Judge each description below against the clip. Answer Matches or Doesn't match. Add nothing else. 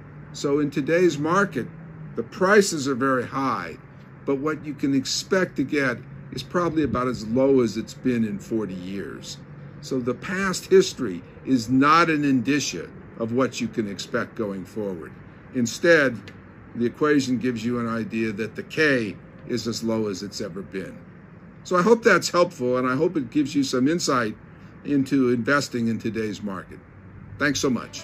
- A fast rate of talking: Doesn't match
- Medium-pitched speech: Doesn't match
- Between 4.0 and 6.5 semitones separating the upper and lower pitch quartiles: Matches